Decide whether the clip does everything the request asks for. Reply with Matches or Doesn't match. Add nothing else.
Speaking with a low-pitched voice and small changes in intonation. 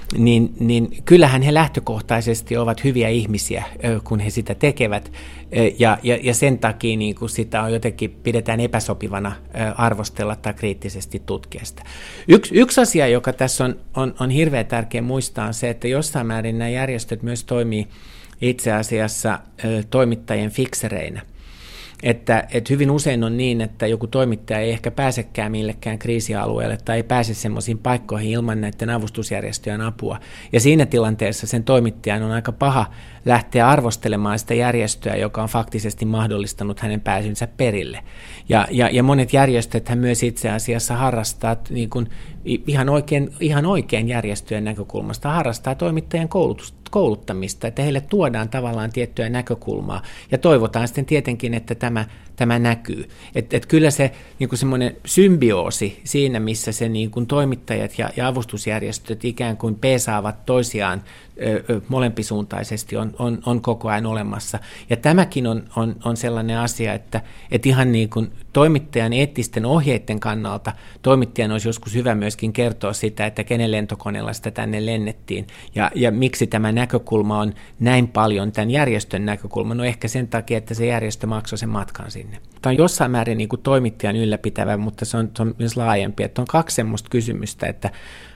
Matches